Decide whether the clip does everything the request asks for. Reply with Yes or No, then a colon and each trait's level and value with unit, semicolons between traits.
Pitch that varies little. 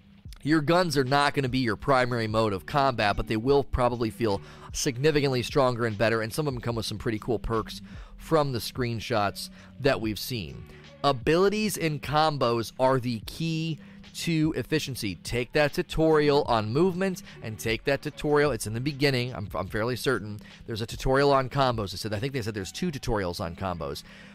No: average, 5.3 semitones